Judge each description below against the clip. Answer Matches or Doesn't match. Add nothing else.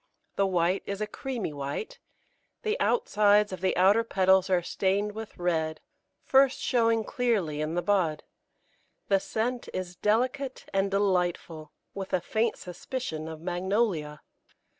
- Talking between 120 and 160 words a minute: Matches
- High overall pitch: Matches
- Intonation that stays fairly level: Doesn't match